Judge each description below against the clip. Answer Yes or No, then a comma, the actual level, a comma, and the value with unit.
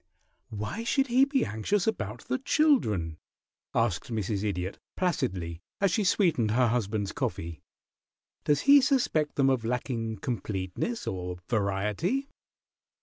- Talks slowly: Yes, slow, 125 wpm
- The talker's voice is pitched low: Yes, low, 120 Hz